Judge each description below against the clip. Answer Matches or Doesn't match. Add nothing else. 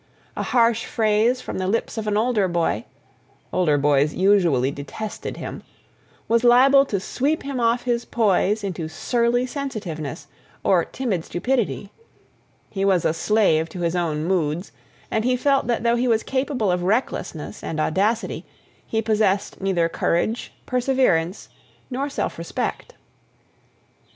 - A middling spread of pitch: Doesn't match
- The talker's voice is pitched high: Matches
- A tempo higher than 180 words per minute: Doesn't match